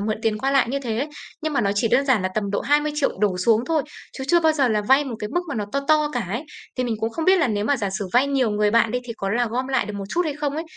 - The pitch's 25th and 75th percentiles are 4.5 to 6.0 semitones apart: Yes, average, 5.1 semitones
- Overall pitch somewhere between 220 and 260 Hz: Yes, very high, 250 Hz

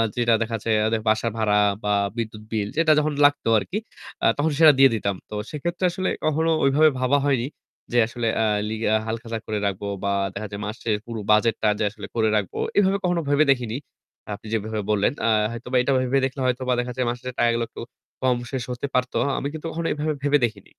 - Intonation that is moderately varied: Yes, average, 4.6 semitones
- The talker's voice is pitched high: No, low, 120 Hz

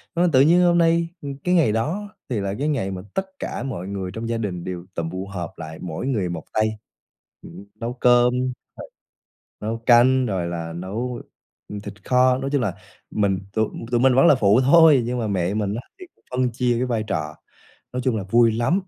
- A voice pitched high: No, low, 115 Hz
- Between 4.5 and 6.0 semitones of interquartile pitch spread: Yes, average, 5.1 semitones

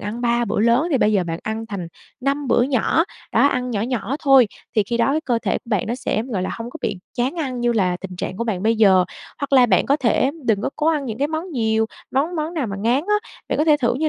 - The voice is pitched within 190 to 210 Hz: No, high, 240 Hz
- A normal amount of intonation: Yes, average, 4.3 semitones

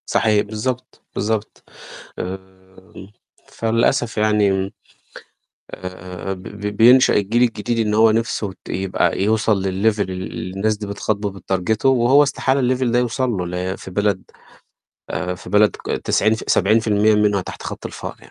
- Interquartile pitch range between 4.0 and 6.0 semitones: No, average, 2.9 semitones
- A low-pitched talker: Yes, low, 105 Hz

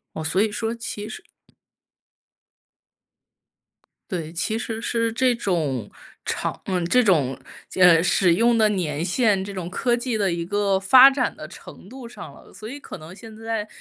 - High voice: Yes, high, 205 Hz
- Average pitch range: Yes, average, 4.6 semitones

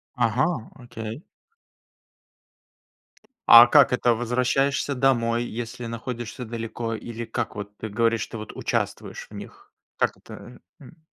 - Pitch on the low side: Yes, low, 120 Hz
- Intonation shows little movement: Yes, narrow, 1.8 semitones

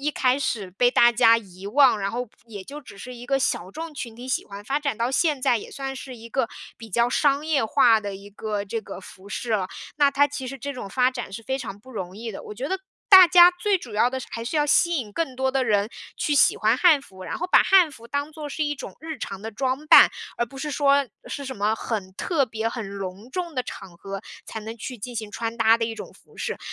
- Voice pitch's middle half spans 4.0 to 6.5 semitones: Yes, average, 4.7 semitones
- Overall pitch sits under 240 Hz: No, high, 245 Hz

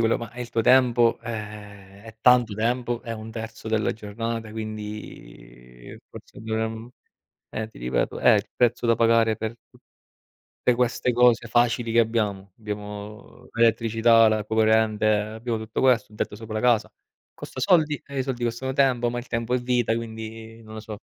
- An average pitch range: No, narrow, 1.8 semitones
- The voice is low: Yes, low, 115 Hz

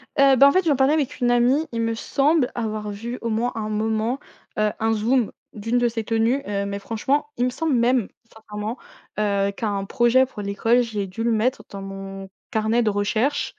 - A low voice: No, high, 225 Hz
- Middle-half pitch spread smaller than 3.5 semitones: Yes, average, 3.0 semitones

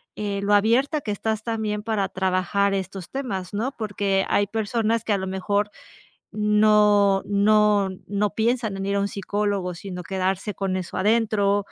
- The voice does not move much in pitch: Yes, narrow, 1.8 semitones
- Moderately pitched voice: No, high, 205 Hz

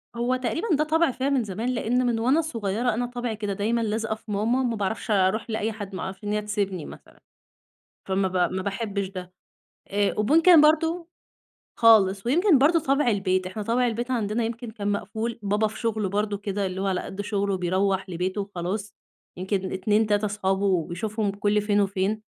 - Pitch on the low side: No, high, 210 Hz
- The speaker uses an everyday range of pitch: Yes, average, 3.2 semitones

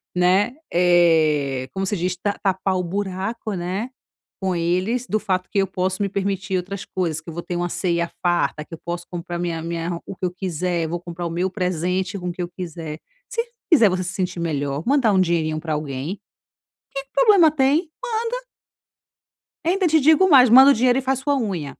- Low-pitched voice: No, medium, 185 Hz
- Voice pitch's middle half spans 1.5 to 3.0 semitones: No, average, 3.6 semitones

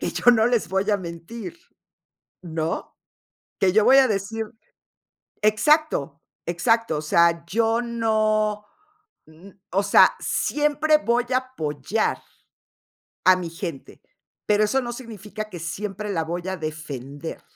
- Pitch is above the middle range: Yes, high, 210 Hz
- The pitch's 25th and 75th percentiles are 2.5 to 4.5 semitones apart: No, wide, 5.4 semitones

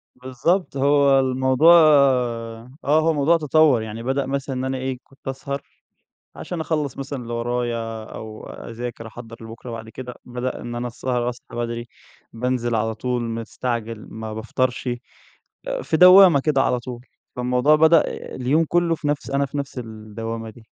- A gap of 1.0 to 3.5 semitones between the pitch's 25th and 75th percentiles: Yes, average, 3.2 semitones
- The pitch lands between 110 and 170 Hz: Yes, low, 125 Hz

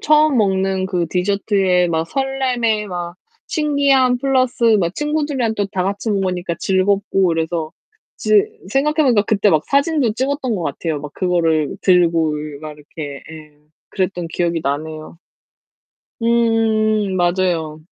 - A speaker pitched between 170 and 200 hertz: Yes, high, 190 Hz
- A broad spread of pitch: Yes, wide, 6.1 semitones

